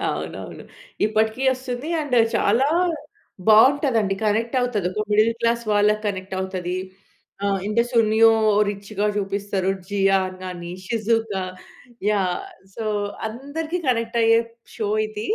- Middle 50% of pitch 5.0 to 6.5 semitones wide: No, average, 2.9 semitones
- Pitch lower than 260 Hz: Yes, high, 215 Hz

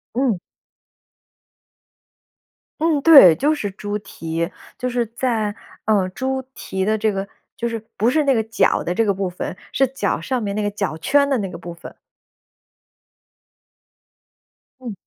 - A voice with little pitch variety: No, average, 5.0 semitones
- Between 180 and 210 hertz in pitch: No, high, 220 Hz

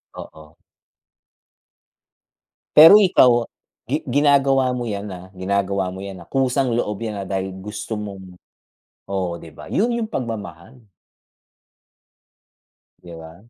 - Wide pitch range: Yes, wide, 5.7 semitones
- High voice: No, low, 105 Hz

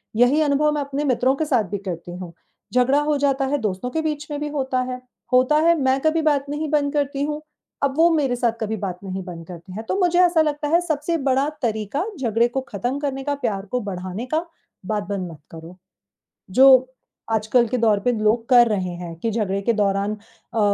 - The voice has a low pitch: No, very high, 255 Hz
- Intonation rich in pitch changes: Yes, wide, 5.9 semitones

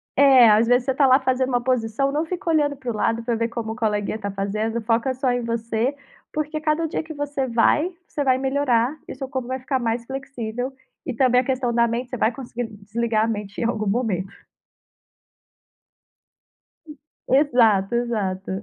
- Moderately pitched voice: No, high, 245 Hz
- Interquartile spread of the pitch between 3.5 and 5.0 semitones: No, average, 2.9 semitones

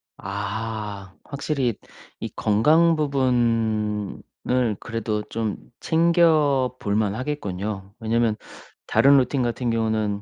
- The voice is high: No, low, 115 Hz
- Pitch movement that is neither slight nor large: Yes, average, 4.3 semitones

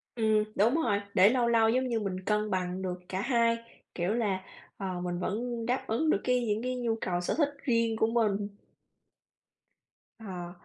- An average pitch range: Yes, average, 3.8 semitones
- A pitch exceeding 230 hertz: No, high, 220 Hz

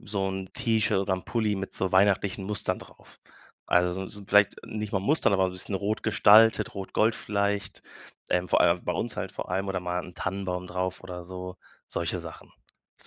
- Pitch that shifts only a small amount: Yes, narrow, 1.9 semitones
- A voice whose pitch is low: Yes, very low, 95 Hz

